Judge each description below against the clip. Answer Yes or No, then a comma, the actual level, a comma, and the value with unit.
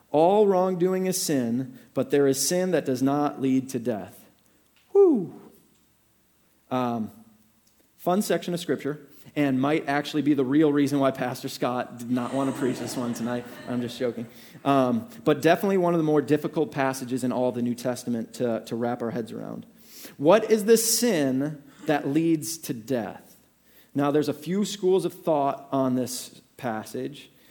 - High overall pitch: No, medium, 140 Hz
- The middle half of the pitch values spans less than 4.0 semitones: No, average, 4.9 semitones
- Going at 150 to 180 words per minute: Yes, average, 170 wpm